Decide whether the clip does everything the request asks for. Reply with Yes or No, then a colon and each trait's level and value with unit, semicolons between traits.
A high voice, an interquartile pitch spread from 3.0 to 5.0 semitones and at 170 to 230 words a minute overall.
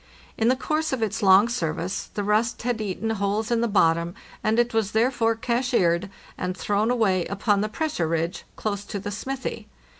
Yes: high, 215 Hz; average, 3.5 semitones; average, 185 wpm